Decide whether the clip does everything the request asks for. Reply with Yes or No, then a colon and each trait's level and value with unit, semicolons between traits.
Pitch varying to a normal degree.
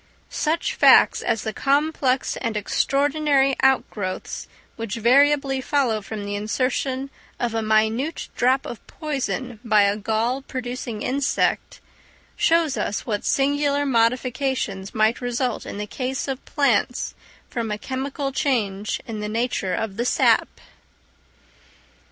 Yes: average, 4.0 semitones